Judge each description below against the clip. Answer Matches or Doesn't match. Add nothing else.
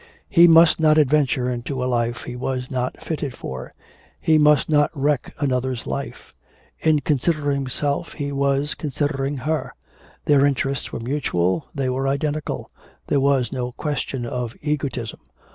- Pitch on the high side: Doesn't match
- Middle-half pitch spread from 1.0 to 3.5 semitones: Matches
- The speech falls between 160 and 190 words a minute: Doesn't match